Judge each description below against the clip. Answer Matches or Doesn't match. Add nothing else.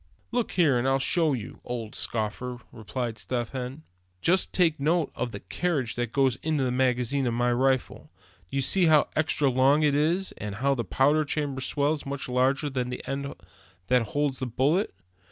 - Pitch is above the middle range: Doesn't match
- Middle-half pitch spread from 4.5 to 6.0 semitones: Doesn't match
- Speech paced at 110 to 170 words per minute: Doesn't match